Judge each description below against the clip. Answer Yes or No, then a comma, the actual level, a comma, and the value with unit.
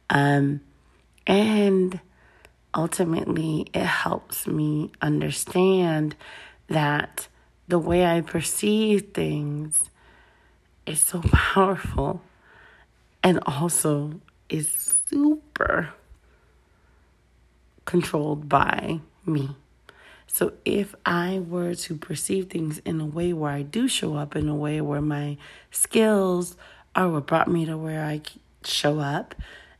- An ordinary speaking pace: No, slow, 105 wpm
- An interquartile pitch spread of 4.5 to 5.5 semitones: No, average, 3.6 semitones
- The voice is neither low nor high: Yes, medium, 160 Hz